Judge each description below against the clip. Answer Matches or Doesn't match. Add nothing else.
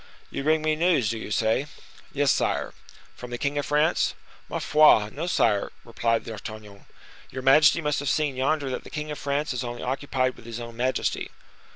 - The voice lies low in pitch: Matches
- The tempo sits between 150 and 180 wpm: Doesn't match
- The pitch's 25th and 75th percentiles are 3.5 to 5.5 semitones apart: Matches